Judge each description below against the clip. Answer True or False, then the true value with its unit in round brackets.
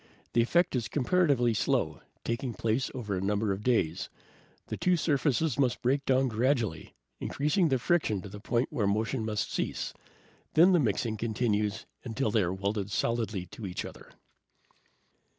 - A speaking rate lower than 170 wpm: True (160 wpm)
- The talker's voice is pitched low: True (115 Hz)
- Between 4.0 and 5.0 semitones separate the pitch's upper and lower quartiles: True (4.4 semitones)